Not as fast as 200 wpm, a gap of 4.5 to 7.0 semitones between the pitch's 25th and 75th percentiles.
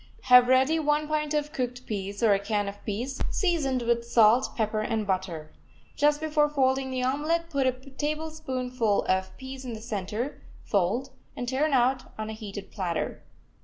Yes: average, 170 wpm; average, 5.1 semitones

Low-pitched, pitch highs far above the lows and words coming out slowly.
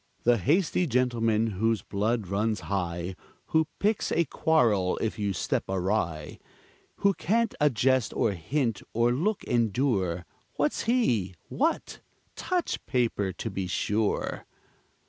Yes: low, 115 Hz; wide, 7.0 semitones; slow, 125 wpm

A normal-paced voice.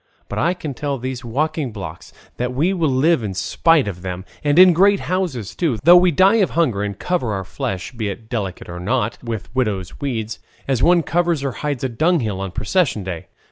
No: fast, 215 wpm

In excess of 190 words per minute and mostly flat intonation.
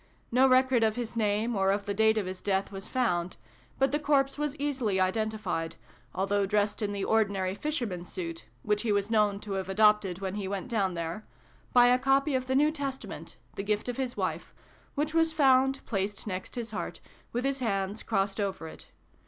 No: average, 200 wpm; average, 4.8 semitones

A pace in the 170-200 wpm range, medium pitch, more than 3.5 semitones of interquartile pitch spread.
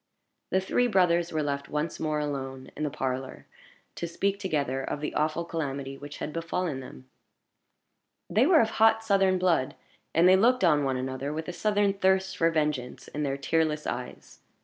Yes: average, 180 wpm; medium, 155 Hz; average, 5.2 semitones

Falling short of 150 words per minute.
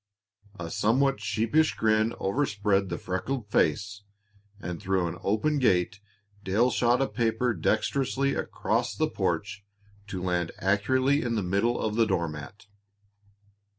Yes: slow, 135 wpm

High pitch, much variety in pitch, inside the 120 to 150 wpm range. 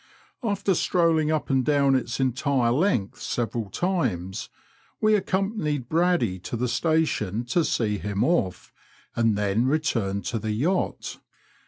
No: low, 130 Hz; wide, 7.1 semitones; slow, 135 wpm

